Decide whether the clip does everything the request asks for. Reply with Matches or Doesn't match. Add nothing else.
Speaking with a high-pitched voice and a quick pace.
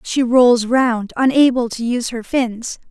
Doesn't match